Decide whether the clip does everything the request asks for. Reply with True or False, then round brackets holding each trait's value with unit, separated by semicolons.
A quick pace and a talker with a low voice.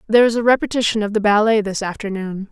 False (215 wpm; 215 Hz)